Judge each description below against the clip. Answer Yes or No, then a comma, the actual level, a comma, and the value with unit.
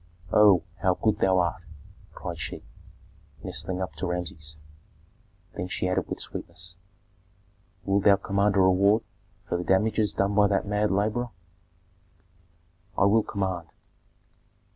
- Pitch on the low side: Yes, very low, 95 Hz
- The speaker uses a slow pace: Yes, slow, 130 wpm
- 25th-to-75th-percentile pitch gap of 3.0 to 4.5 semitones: No, narrow, 2.4 semitones